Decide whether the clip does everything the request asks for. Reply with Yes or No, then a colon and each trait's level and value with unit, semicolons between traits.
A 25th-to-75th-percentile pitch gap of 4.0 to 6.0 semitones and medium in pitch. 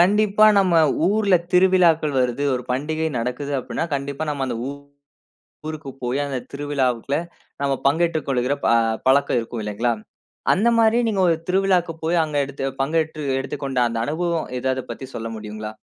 Yes: average, 5.0 semitones; medium, 145 Hz